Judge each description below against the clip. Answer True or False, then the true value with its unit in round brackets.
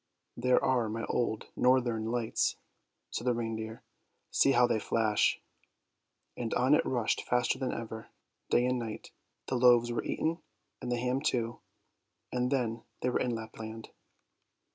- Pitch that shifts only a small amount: True (1.9 semitones)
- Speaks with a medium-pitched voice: False (120 Hz)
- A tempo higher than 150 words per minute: True (160 wpm)